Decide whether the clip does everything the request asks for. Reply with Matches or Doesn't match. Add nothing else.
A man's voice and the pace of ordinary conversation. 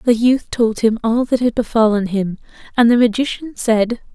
Doesn't match